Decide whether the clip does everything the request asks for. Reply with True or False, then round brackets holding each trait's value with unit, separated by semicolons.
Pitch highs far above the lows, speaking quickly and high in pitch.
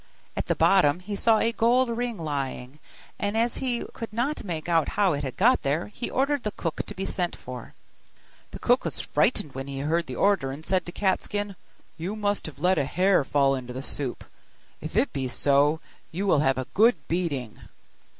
False (6.8 semitones; 210 wpm; 175 Hz)